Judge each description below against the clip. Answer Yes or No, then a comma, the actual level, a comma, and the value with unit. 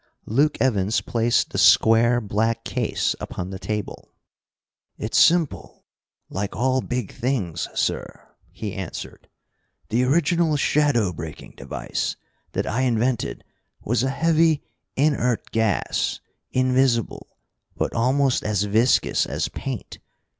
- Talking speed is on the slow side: Yes, slow, 115 wpm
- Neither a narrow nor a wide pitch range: Yes, average, 4.0 semitones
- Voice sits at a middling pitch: No, low, 120 Hz